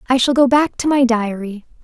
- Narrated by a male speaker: No, female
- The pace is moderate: No, fast, 230 wpm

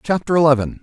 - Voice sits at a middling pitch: Yes, medium, 150 Hz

